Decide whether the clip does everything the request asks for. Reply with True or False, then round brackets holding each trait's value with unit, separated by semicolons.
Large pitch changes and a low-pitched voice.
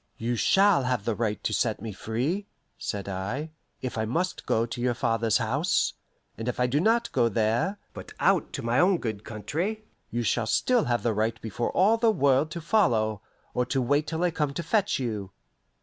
True (7.0 semitones; 125 Hz)